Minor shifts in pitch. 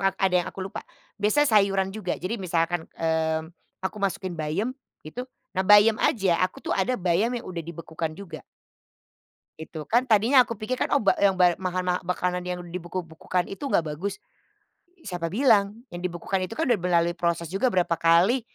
No: average, 3.3 semitones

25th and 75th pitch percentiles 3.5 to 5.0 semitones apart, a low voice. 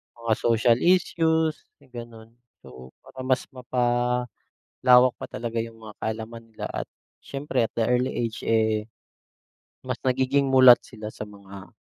No: narrow, 2.6 semitones; low, 120 Hz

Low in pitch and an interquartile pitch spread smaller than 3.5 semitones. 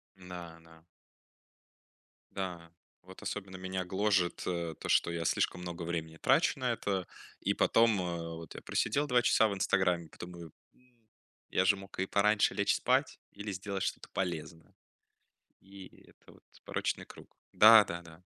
Yes: very low, 95 Hz; average, 3.1 semitones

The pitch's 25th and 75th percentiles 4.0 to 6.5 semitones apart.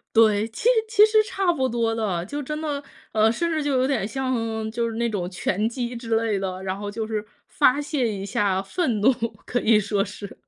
Yes: average, 4.4 semitones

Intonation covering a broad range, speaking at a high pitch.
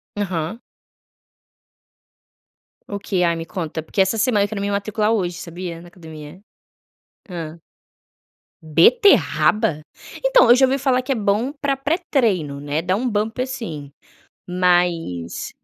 Yes: wide, 5.8 semitones; high, 195 Hz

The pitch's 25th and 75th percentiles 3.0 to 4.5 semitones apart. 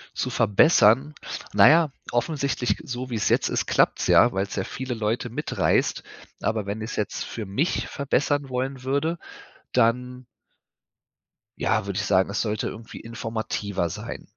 Yes: average, 4.0 semitones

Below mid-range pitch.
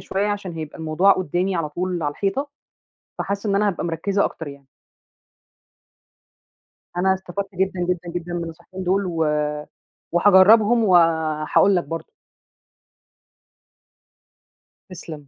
No: medium, 180 Hz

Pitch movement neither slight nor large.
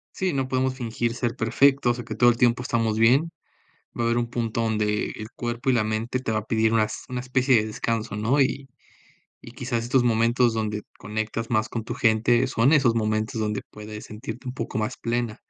No: narrow, 2.2 semitones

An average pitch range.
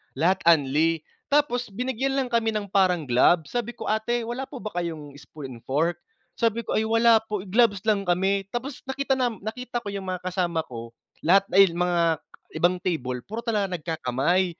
No: wide, 5.7 semitones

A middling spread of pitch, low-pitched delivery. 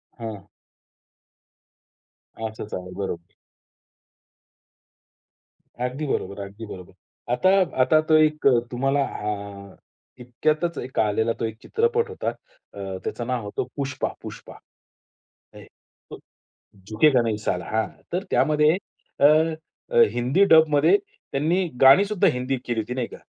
No: wide, 6.3 semitones; low, 125 Hz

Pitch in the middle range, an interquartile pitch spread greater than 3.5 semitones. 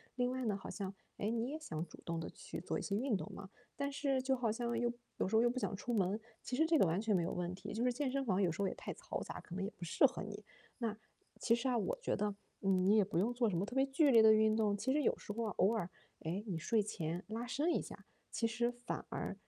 No: high, 220 Hz; average, 4.2 semitones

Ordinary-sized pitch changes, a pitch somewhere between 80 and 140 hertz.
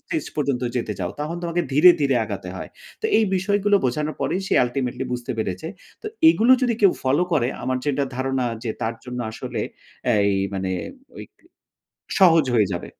No: wide, 6.3 semitones; low, 135 Hz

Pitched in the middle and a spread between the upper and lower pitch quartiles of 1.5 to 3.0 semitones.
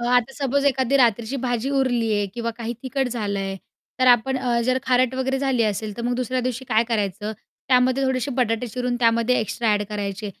No: high, 245 Hz; average, 2.7 semitones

